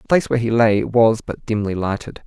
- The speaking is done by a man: Yes, male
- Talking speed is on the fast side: Yes, fast, 240 wpm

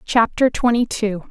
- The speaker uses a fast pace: No, average, 140 wpm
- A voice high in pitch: Yes, high, 225 Hz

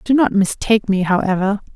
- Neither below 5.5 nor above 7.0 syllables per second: Yes, 5.8 syllables/s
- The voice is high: Yes, high, 205 Hz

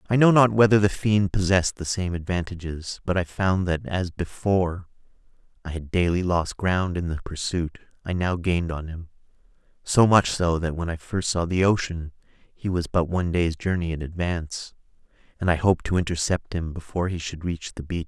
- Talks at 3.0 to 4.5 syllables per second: No, 5.3 syllables/s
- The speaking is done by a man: Yes, male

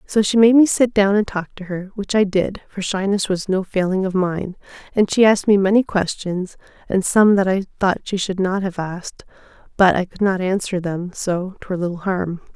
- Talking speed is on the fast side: Yes, fast, 220 wpm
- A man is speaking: No, female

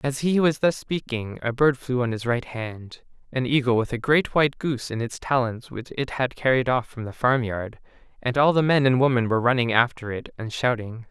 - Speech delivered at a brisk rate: Yes, fast, 220 wpm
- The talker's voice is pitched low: Yes, low, 125 Hz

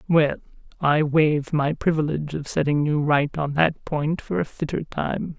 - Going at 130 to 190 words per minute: Yes, average, 180 wpm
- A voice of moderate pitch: Yes, medium, 150 Hz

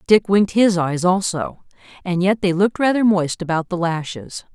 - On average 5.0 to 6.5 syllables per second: Yes, 5.1 syllables/s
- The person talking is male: No, female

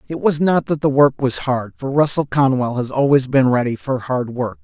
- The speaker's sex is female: No, male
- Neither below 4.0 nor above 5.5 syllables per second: Yes, 5.0 syllables/s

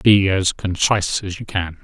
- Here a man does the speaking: Yes, male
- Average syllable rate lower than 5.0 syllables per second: Yes, 4.5 syllables/s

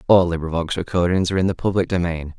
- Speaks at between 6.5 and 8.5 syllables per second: Yes, 6.8 syllables/s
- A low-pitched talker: Yes, very low, 90 Hz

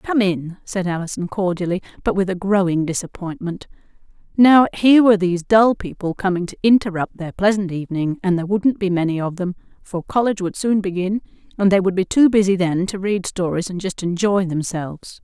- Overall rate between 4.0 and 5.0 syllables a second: No, 5.6 syllables/s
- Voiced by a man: No, female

